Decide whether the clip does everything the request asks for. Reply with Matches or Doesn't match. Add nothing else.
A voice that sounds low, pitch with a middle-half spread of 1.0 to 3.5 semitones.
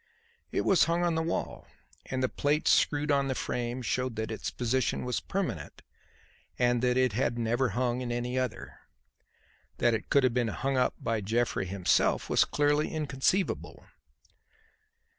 Matches